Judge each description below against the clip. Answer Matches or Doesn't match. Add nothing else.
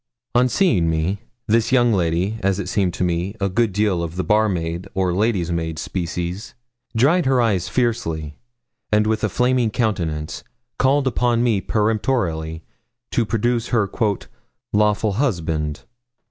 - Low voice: Matches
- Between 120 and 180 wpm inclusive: Matches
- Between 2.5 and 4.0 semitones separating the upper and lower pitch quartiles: Doesn't match